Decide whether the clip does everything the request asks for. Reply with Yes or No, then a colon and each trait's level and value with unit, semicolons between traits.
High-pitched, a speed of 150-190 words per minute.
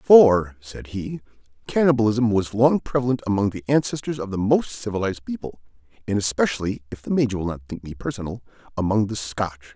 No: low, 110 Hz; average, 170 wpm